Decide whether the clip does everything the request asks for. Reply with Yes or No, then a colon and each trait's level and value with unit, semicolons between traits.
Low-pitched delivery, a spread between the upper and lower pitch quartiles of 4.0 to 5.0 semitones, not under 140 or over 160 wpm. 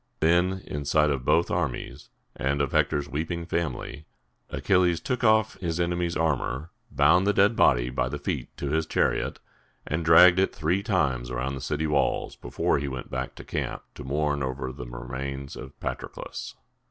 No: very low, 75 Hz; average, 4.3 semitones; average, 175 wpm